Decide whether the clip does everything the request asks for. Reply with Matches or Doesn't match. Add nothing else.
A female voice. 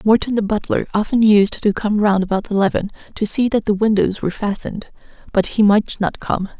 Matches